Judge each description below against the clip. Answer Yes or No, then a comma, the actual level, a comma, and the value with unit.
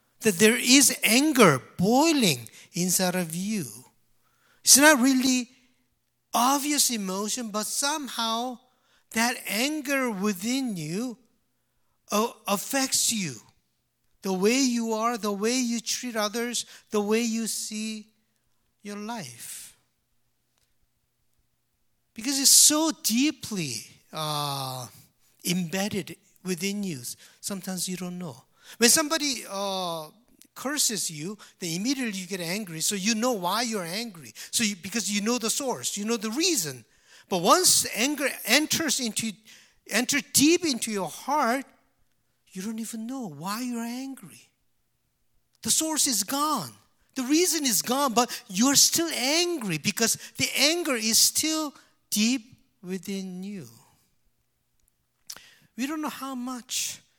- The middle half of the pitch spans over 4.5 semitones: Yes, average, 5.1 semitones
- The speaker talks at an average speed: No, slow, 125 wpm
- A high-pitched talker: Yes, high, 225 Hz